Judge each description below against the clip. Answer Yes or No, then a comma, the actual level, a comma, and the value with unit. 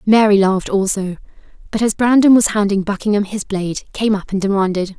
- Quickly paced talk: No, average, 180 wpm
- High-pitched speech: Yes, high, 205 Hz